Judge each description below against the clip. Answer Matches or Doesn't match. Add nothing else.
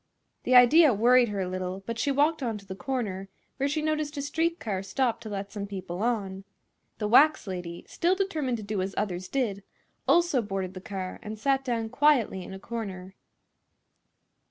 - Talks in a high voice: Matches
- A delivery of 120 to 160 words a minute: Doesn't match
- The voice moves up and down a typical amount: Doesn't match